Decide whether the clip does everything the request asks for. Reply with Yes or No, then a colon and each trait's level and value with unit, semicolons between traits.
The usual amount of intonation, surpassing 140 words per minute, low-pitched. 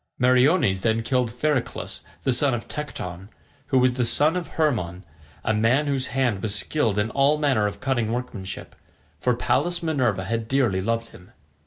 Yes: average, 4.4 semitones; average, 170 wpm; low, 125 Hz